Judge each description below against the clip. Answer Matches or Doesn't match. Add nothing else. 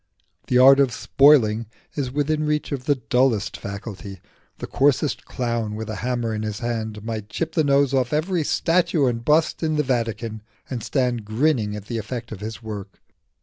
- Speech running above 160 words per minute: Matches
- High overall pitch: Doesn't match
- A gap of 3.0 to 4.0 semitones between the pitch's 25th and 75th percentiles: Doesn't match